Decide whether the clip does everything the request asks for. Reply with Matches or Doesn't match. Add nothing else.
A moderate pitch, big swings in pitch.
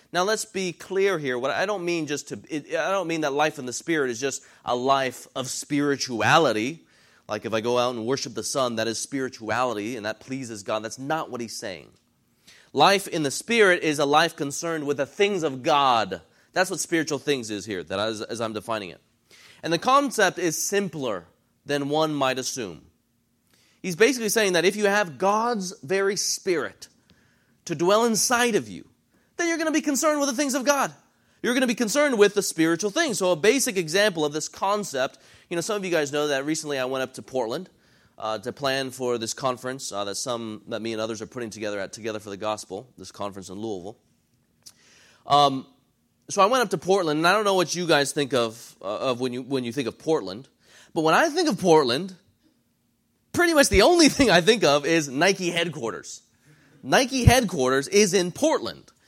Matches